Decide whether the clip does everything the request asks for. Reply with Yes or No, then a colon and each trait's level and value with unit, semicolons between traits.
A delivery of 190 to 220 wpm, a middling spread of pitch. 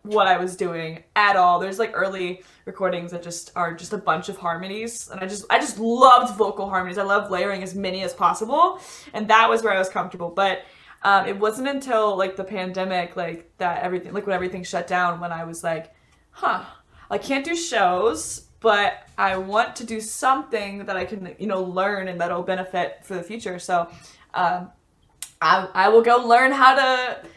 Yes: fast, 205 wpm; average, 3.3 semitones